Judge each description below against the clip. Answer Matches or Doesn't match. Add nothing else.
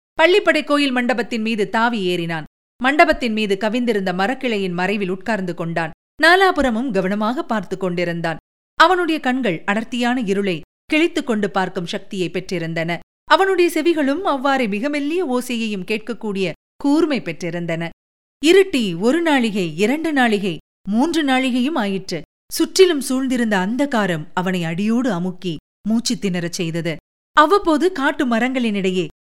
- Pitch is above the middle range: Matches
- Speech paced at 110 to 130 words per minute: Matches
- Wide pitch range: Matches